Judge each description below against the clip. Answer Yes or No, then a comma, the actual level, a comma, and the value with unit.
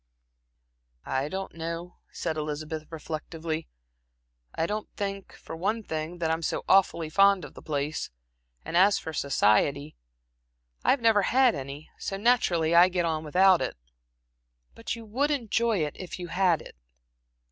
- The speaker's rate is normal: Yes, average, 160 wpm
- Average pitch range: Yes, average, 4.1 semitones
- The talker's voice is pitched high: No, medium, 170 Hz